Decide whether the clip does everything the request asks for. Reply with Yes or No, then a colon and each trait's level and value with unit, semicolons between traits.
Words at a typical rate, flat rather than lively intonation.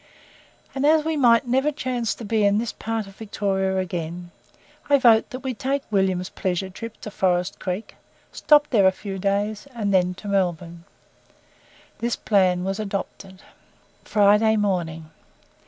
No: average, 155 wpm; average, 3.6 semitones